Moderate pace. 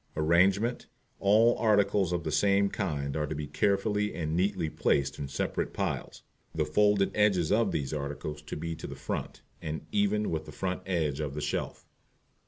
Yes: average, 180 wpm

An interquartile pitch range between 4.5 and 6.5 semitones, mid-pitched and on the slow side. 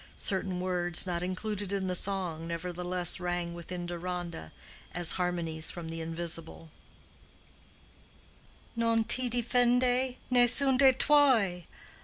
Yes: average, 5.1 semitones; medium, 180 Hz; slow, 110 wpm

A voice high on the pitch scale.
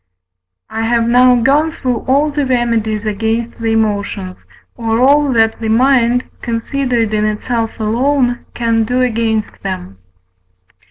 Yes: high, 230 Hz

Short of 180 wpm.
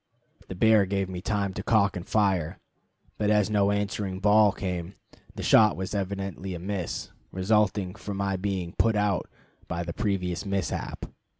Yes: average, 165 wpm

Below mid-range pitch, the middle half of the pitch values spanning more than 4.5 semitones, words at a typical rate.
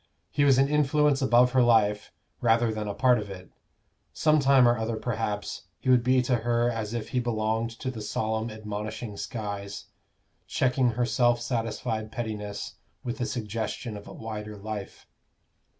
No: low, 115 Hz; narrow, 2.6 semitones; average, 165 wpm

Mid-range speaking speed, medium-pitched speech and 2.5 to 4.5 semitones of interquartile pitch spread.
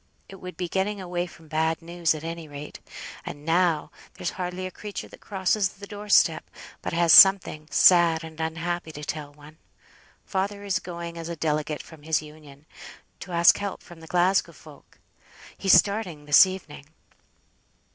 Yes: average, 170 wpm; medium, 170 Hz; average, 3.0 semitones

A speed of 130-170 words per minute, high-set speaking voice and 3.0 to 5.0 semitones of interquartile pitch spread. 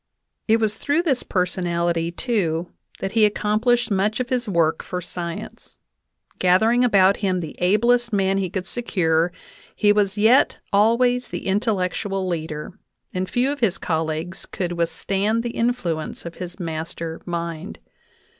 Yes: average, 150 wpm; high, 195 Hz; average, 4.7 semitones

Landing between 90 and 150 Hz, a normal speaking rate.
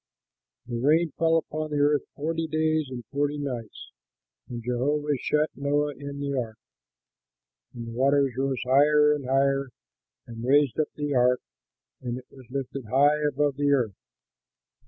Yes: medium, 140 Hz; average, 155 wpm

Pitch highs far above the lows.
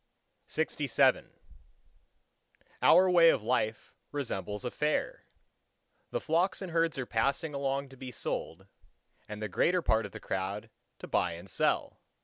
Yes: wide, 7.5 semitones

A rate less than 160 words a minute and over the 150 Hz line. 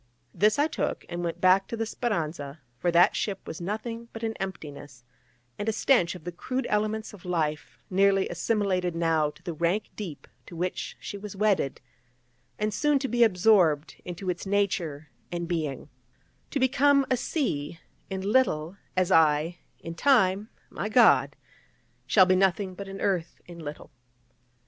No: average, 165 wpm; medium, 185 Hz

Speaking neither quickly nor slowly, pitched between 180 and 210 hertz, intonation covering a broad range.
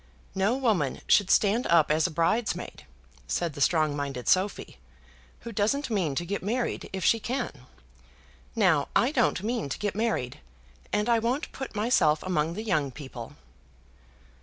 Yes: average, 160 wpm; high, 190 Hz; wide, 6.8 semitones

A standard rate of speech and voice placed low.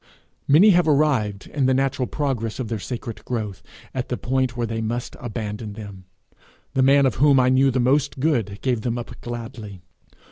Yes: average, 185 wpm; low, 125 Hz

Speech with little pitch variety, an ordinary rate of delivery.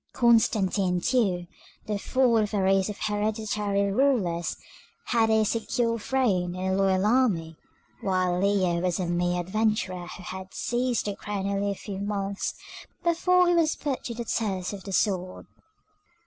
No: average, 3.5 semitones; average, 160 wpm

